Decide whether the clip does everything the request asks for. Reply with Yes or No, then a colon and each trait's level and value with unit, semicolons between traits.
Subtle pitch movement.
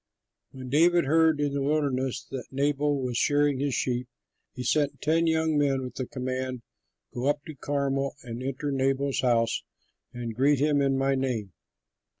Yes: narrow, 2.2 semitones